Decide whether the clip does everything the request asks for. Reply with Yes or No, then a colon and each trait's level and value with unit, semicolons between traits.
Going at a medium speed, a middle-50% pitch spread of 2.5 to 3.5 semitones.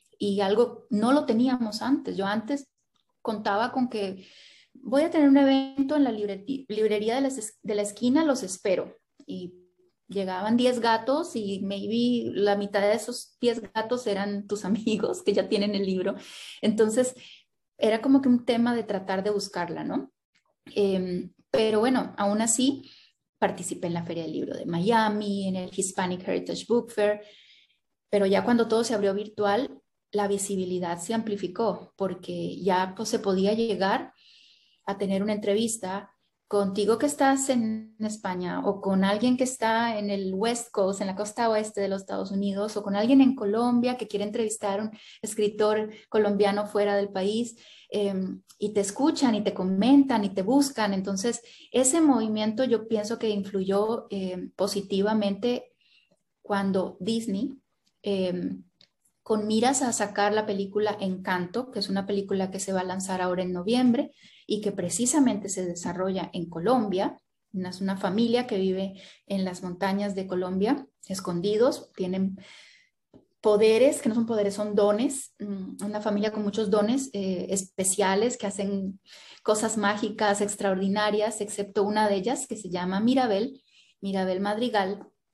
Yes: average, 155 wpm; average, 2.9 semitones